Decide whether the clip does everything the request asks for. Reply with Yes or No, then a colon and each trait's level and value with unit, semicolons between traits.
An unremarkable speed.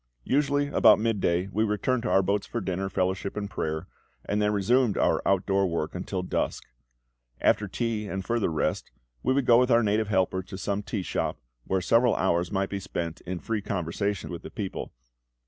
Yes: average, 195 wpm